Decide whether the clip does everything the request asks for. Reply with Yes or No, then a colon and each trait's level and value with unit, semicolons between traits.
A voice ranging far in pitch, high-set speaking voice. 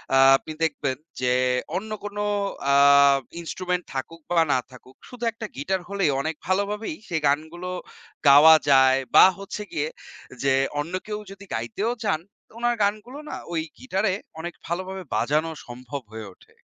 No: wide, 6.1 semitones; medium, 170 Hz